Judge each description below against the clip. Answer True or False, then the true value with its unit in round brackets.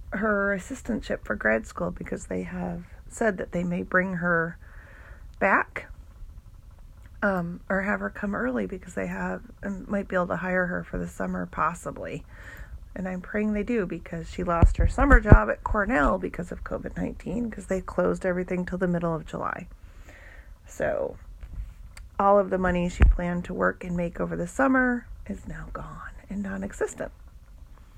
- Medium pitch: True (175 Hz)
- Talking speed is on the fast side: False (175 wpm)